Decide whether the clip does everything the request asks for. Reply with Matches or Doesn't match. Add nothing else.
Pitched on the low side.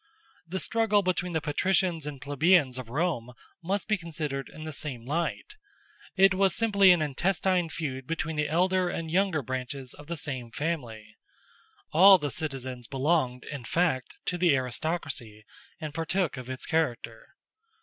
Doesn't match